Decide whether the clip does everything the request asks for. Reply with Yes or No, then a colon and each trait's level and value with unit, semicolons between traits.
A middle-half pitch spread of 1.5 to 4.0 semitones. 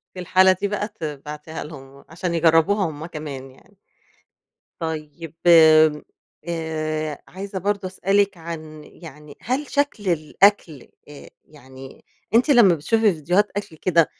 No: average, 4.4 semitones